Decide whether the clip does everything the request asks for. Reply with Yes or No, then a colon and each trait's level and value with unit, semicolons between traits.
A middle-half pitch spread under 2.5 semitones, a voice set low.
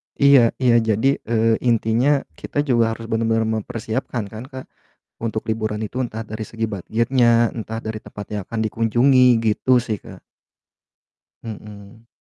Yes: narrow, 1.9 semitones; low, 115 Hz